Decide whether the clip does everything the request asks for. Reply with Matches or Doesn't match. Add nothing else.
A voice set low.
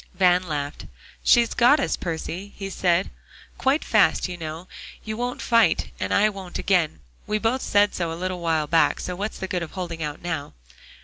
Doesn't match